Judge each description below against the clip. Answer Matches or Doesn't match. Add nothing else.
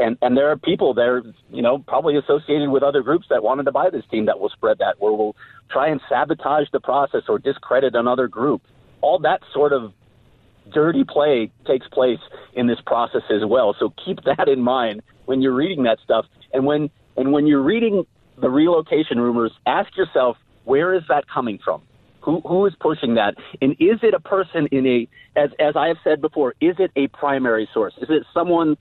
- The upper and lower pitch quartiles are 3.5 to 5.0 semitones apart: Matches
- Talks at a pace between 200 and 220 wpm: Matches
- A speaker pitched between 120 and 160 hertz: Matches